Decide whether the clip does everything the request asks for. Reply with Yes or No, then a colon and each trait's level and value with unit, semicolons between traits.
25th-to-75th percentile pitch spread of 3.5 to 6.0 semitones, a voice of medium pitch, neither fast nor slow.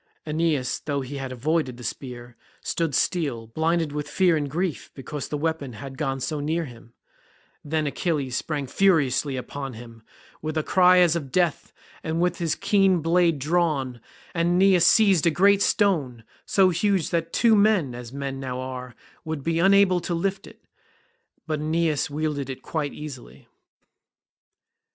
Yes: average, 4.3 semitones; medium, 155 Hz; average, 160 wpm